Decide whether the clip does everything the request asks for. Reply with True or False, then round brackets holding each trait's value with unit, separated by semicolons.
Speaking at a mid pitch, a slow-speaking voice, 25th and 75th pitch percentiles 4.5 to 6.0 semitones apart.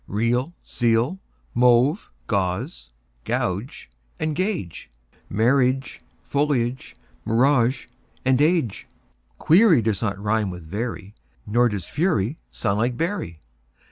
False (120 Hz; 95 wpm; 5.6 semitones)